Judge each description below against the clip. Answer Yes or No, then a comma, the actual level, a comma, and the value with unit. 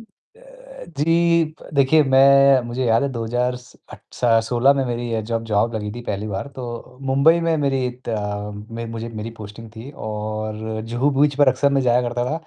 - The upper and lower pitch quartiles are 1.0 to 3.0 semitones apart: No, average, 3.7 semitones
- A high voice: No, low, 120 Hz